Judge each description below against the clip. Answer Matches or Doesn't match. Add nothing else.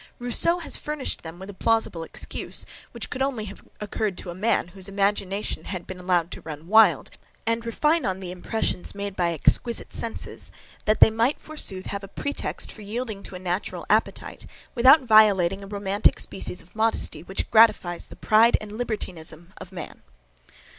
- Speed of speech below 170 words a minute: Doesn't match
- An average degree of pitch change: Matches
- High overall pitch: Matches